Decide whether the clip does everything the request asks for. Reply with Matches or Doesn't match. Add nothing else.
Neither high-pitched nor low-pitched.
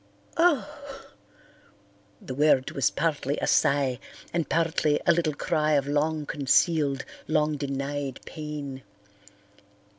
Matches